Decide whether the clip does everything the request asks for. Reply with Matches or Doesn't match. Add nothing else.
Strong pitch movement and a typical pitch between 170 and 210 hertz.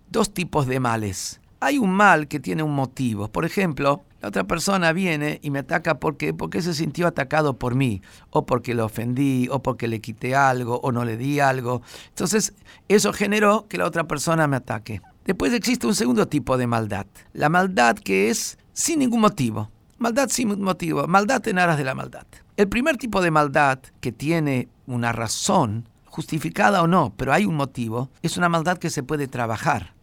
Doesn't match